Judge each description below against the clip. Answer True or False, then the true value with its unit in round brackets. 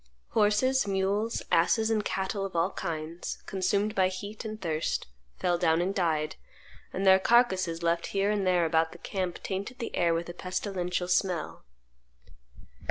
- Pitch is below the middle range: False (190 Hz)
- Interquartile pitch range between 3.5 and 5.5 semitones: False (3.1 semitones)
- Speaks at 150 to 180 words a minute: True (160 wpm)